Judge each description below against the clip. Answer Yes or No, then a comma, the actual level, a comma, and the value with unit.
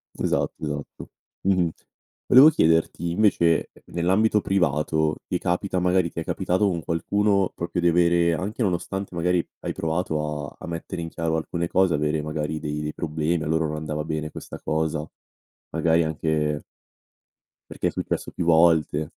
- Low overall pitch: Yes, very low, 85 Hz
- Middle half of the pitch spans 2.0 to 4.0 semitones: Yes, narrow, 2.5 semitones